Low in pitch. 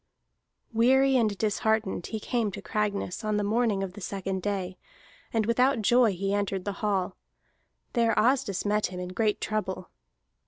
No: high, 210 Hz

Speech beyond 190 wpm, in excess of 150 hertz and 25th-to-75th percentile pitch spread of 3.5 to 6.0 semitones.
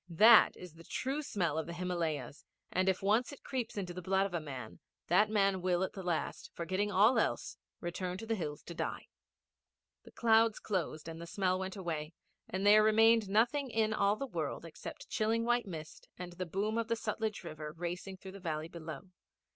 Yes: average, 200 wpm; high, 190 Hz; average, 4.1 semitones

